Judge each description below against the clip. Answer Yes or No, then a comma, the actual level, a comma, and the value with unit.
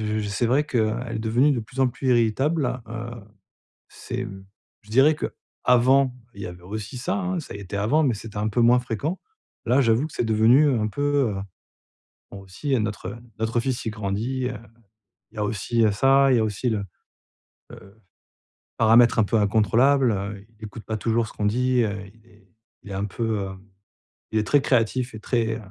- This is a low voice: Yes, low, 115 Hz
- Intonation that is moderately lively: Yes, average, 3.2 semitones